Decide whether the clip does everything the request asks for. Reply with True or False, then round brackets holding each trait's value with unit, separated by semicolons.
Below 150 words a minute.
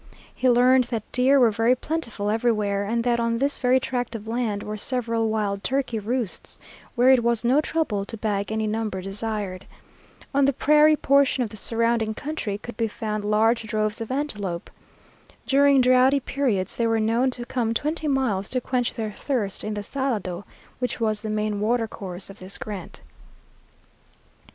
False (175 wpm)